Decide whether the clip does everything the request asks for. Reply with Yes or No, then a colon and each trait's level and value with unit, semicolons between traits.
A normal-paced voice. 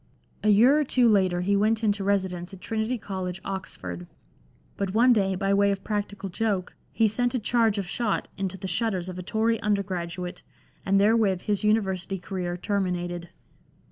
Yes: average, 170 wpm